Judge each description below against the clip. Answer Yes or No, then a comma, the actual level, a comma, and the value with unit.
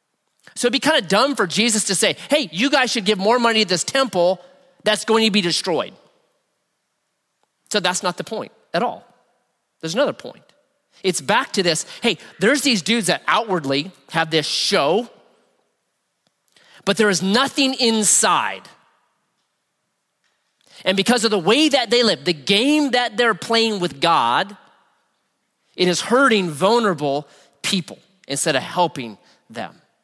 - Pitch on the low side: No, high, 210 Hz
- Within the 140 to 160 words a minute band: Yes, average, 155 wpm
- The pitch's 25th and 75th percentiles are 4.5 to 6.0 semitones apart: Yes, average, 5.2 semitones